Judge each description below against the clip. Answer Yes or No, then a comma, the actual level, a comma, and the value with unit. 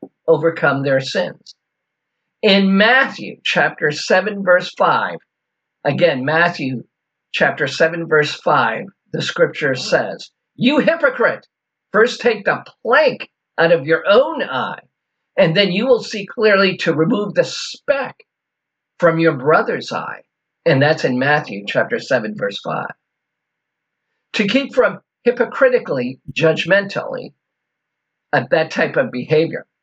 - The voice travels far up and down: Yes, wide, 7.1 semitones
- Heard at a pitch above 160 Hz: Yes, medium, 185 Hz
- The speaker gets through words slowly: Yes, slow, 125 wpm